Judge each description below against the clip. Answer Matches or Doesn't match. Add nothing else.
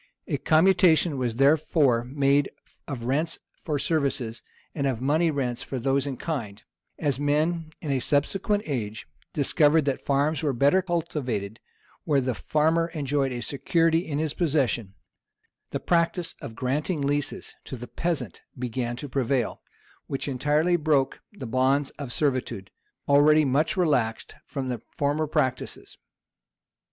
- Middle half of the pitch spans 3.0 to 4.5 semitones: Matches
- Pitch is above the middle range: Doesn't match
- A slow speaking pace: Doesn't match